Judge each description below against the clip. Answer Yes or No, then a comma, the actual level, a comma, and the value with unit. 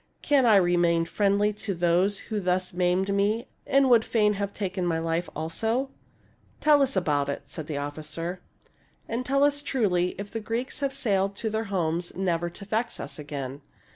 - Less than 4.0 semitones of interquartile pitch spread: No, average, 4.7 semitones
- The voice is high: Yes, high, 195 Hz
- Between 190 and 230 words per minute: Yes, average, 200 wpm